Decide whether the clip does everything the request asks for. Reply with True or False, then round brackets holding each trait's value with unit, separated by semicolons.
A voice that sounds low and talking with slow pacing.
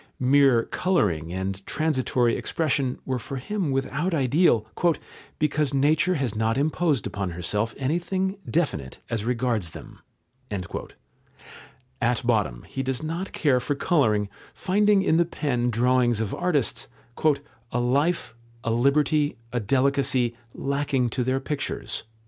True (130 Hz; 125 wpm)